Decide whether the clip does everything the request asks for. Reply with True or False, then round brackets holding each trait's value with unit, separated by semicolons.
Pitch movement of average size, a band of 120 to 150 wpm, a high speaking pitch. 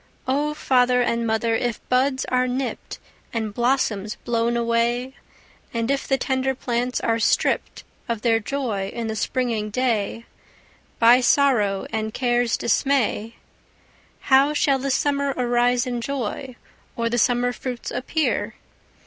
False (2.3 semitones; 135 wpm; 245 Hz)